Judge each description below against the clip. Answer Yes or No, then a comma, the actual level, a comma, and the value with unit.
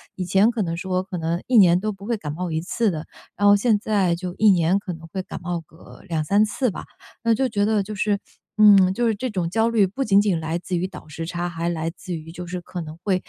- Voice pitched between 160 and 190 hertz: Yes, medium, 185 Hz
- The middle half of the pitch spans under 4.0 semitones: Yes, average, 3.5 semitones